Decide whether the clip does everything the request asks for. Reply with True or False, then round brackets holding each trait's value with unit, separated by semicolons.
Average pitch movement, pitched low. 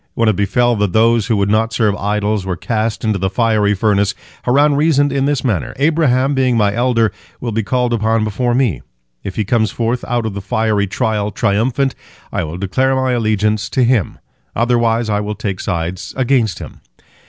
True (3.2 semitones; 110 Hz)